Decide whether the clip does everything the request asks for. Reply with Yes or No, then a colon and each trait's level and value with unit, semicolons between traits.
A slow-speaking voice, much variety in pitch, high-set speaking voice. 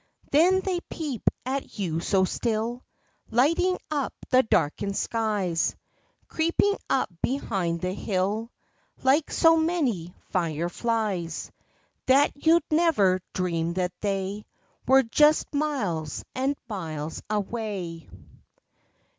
Yes: slow, 105 wpm; wide, 7.7 semitones; high, 220 Hz